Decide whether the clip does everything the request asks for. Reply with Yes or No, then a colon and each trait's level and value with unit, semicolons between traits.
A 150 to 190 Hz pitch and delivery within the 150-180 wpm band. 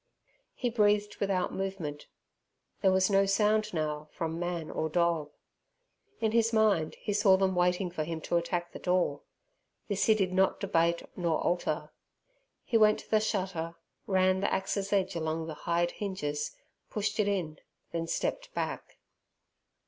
Yes: medium, 185 Hz; average, 155 wpm